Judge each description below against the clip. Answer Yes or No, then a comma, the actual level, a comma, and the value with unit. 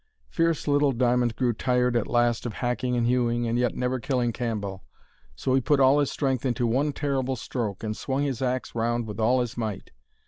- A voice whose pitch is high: No, low, 125 Hz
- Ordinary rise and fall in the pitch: No, narrow, 2.1 semitones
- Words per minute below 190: No, fast, 205 wpm